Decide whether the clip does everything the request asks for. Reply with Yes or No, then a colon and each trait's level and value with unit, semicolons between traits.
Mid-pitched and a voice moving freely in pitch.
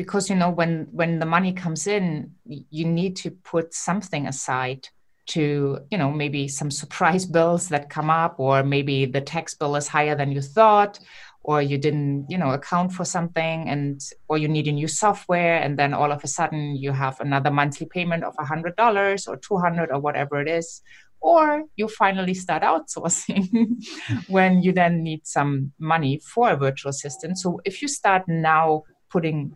No: medium, 160 Hz; average, 4.0 semitones